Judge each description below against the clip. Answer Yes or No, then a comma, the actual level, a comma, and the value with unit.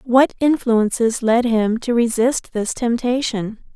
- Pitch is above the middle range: Yes, high, 235 Hz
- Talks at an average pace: No, slow, 130 wpm